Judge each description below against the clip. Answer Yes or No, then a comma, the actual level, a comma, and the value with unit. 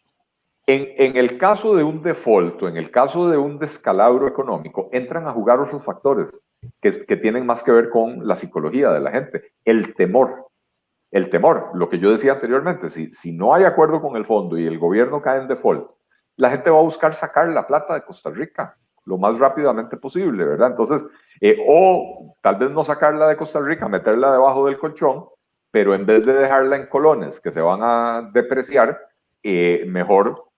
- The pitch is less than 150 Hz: Yes, low, 135 Hz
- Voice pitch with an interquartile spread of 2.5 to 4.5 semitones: No, average, 5.2 semitones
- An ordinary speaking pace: No, fast, 195 wpm